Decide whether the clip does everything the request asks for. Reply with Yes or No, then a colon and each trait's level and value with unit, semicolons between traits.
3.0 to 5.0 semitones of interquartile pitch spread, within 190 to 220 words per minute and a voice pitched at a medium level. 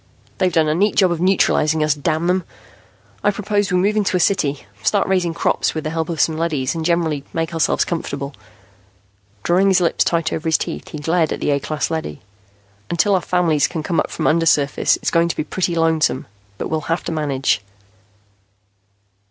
No: narrow, 2.6 semitones; average, 200 wpm; medium, 165 Hz